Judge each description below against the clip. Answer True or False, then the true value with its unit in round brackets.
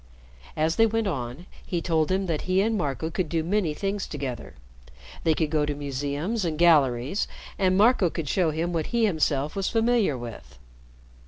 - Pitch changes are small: False (4.9 semitones)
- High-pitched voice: False (165 Hz)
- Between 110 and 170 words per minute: False (180 wpm)